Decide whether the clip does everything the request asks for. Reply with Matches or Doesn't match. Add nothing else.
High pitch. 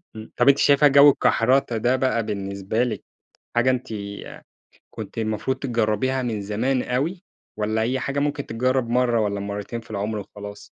Doesn't match